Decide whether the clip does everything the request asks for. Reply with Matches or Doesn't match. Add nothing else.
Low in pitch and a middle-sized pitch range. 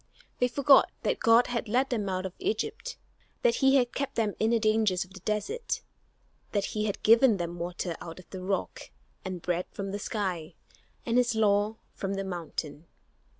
Doesn't match